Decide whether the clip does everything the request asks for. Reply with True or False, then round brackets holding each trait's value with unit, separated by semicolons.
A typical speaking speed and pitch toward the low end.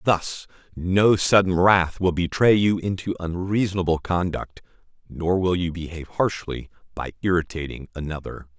False (125 wpm; 90 Hz)